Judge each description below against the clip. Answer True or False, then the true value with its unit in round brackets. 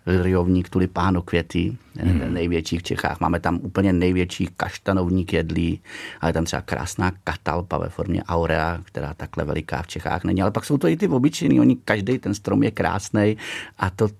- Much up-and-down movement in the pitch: False (2.7 semitones)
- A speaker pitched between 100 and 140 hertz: False (90 Hz)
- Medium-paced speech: False (180 wpm)